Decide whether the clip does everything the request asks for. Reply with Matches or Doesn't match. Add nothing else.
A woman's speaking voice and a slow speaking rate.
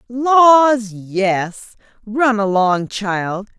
Matches